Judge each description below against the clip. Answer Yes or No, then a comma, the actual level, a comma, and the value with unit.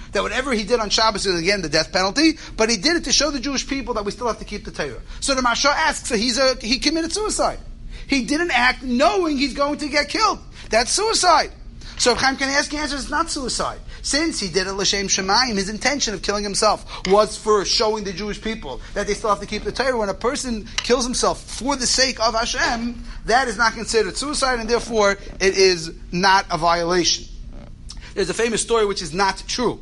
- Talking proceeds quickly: Yes, fast, 225 wpm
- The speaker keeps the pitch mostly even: No, average, 5.2 semitones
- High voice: Yes, high, 230 Hz